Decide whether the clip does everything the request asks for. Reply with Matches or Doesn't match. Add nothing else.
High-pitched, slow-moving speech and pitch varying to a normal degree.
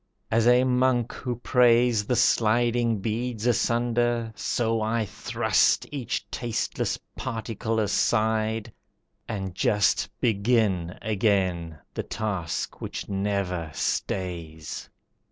Doesn't match